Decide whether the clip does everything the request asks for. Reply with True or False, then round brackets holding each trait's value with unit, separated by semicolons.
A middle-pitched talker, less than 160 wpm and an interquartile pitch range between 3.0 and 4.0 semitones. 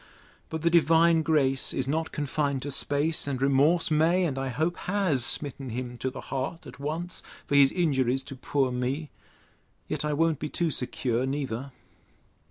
False (145 Hz; 175 wpm; 3.4 semitones)